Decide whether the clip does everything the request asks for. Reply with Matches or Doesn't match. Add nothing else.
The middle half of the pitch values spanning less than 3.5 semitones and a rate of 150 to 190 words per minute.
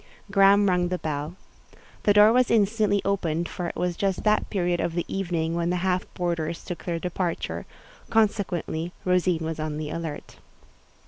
Matches